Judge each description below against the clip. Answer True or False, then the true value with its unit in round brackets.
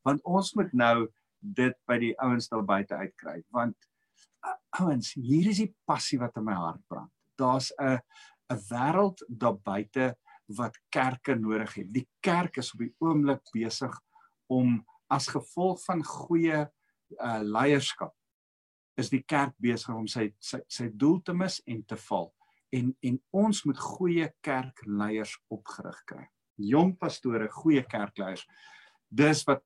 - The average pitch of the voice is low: True (130 Hz)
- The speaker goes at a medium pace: True (150 wpm)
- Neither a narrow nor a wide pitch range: False (5.8 semitones)